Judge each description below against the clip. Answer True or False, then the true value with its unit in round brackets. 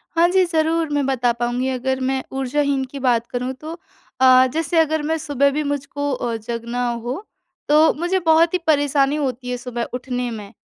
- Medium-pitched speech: False (275 Hz)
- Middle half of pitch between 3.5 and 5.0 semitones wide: True (3.9 semitones)